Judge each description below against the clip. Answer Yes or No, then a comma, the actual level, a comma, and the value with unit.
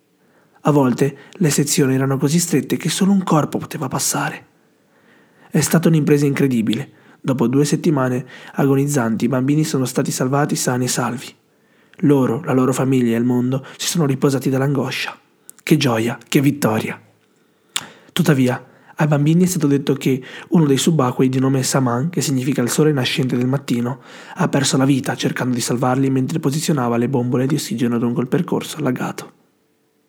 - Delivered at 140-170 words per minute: Yes, average, 160 wpm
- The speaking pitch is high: No, medium, 140 Hz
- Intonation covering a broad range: No, average, 2.9 semitones